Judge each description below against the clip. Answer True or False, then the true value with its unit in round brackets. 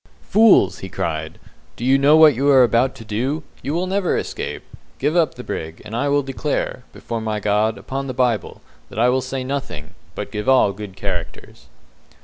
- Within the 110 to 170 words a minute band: False (195 wpm)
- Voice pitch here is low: True (130 Hz)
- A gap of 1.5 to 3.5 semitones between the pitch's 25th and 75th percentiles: False (4.8 semitones)